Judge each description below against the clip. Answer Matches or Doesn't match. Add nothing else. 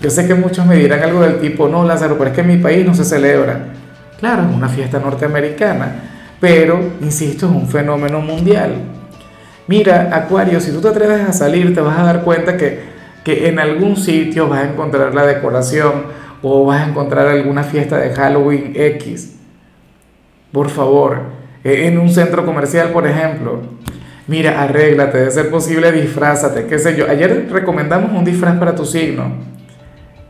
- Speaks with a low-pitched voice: Doesn't match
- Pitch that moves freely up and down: Doesn't match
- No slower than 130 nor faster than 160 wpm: Doesn't match